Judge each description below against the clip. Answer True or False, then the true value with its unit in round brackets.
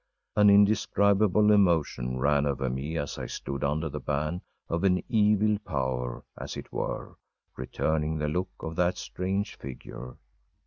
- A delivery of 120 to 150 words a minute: True (145 wpm)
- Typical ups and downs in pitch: False (6.1 semitones)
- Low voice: True (80 Hz)